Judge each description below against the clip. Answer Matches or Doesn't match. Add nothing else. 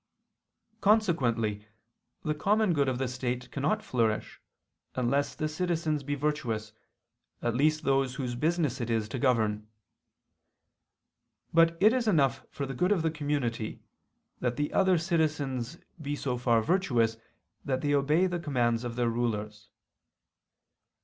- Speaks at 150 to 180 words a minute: Doesn't match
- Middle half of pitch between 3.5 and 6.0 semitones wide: Matches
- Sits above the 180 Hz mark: Doesn't match